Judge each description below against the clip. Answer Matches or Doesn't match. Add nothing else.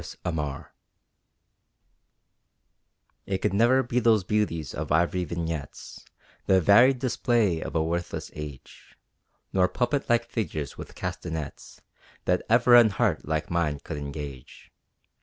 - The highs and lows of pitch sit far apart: Matches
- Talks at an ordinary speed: Doesn't match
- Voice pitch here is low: Matches